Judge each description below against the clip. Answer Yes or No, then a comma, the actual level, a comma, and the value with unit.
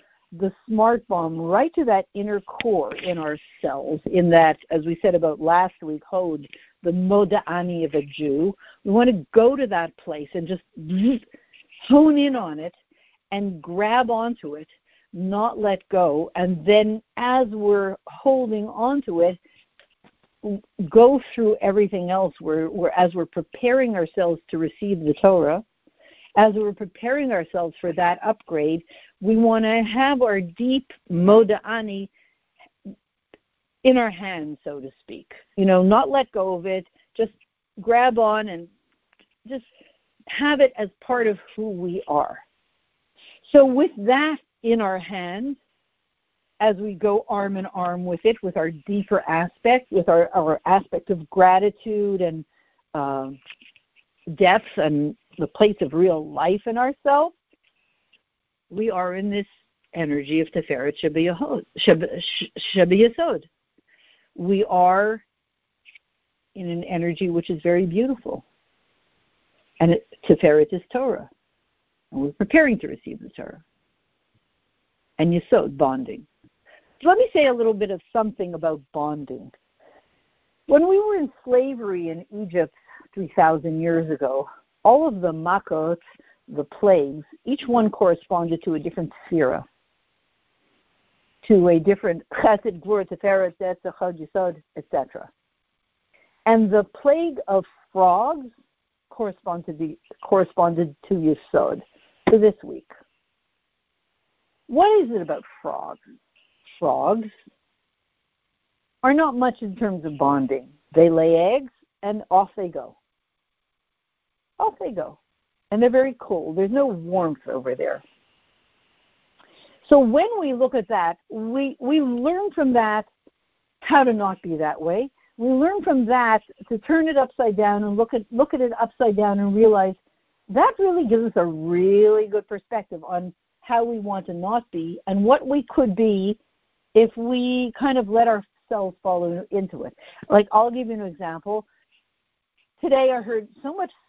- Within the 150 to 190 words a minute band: No, average, 140 wpm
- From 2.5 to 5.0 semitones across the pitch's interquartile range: No, wide, 5.5 semitones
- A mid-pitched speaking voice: No, high, 205 Hz